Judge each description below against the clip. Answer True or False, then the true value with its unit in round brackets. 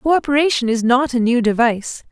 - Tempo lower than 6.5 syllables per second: True (5.9 syllables/s)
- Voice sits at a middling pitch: False (250 Hz)